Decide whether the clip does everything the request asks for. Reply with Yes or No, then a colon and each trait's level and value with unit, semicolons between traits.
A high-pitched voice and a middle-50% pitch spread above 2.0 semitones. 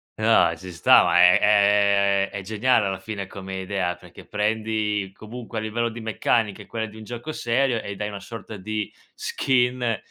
No: low, 105 Hz; narrow, 2.5 semitones